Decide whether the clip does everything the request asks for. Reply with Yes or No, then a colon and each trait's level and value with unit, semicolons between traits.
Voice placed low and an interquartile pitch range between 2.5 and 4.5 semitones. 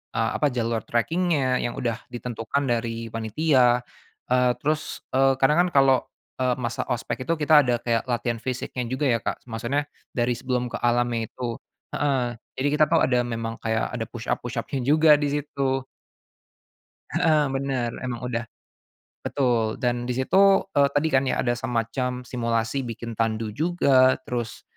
Yes: low, 125 Hz; average, 2.8 semitones